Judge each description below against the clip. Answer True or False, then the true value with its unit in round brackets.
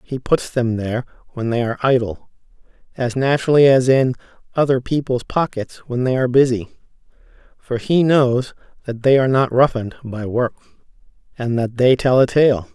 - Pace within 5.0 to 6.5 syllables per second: True (5.3 syllables/s)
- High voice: False (125 Hz)